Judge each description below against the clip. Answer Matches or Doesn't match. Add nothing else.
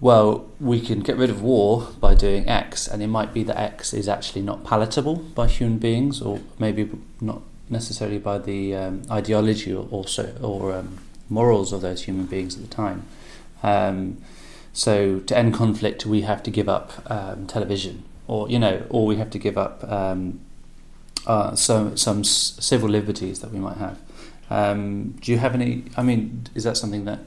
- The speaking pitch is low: Matches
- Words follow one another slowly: Doesn't match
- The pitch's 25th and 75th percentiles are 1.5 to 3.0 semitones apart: Matches